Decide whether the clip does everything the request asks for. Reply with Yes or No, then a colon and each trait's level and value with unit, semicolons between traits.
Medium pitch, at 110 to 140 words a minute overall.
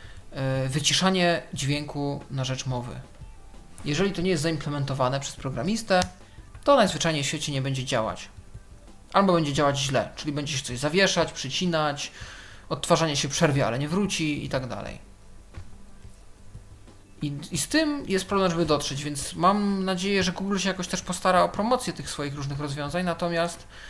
No: medium, 145 Hz; average, 155 wpm